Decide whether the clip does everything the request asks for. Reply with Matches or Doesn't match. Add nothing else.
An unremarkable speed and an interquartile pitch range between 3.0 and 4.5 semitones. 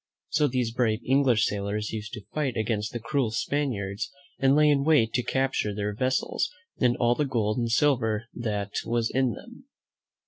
Matches